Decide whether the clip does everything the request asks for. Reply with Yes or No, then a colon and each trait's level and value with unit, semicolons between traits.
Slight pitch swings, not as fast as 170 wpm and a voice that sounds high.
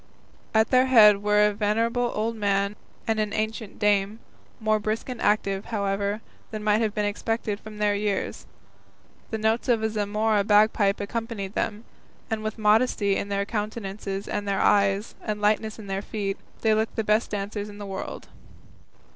No: narrow, 1.4 semitones; average, 175 wpm; high, 210 Hz